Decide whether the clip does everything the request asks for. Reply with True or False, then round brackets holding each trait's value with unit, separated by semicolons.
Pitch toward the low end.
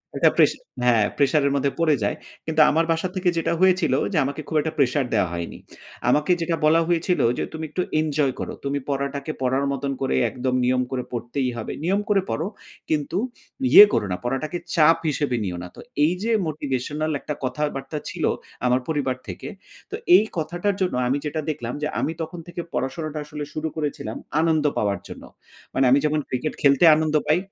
False (150 Hz)